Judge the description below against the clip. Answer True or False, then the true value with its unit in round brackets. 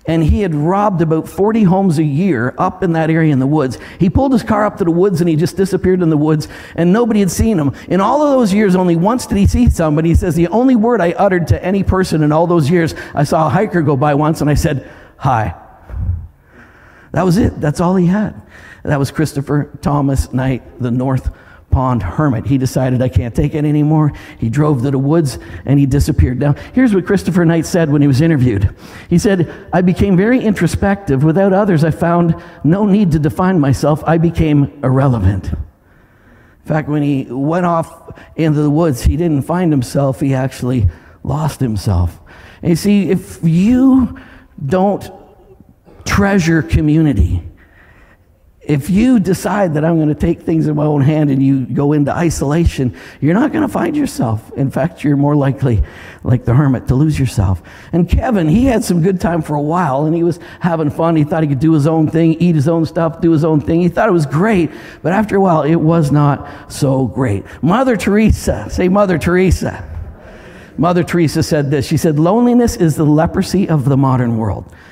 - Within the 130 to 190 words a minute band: False (200 wpm)